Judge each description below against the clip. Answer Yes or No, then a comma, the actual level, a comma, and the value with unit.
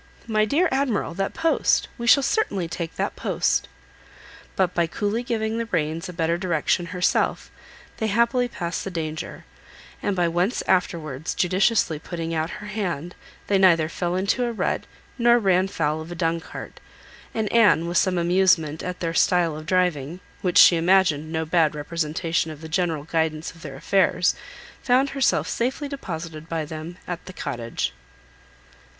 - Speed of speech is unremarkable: Yes, average, 165 wpm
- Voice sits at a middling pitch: Yes, medium, 175 Hz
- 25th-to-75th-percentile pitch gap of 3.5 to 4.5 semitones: Yes, average, 3.9 semitones